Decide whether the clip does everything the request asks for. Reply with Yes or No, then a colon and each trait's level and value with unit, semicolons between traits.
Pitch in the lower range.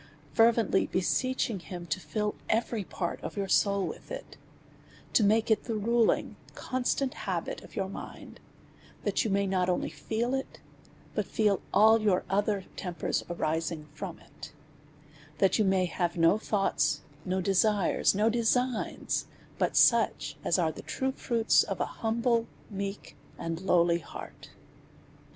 No: high, 200 Hz